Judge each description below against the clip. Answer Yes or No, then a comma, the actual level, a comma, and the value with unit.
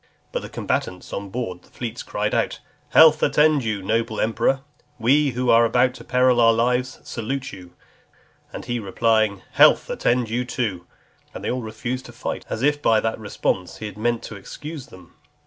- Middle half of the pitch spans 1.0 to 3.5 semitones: Yes, average, 2.8 semitones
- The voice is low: Yes, low, 115 Hz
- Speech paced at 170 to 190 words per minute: Yes, average, 180 wpm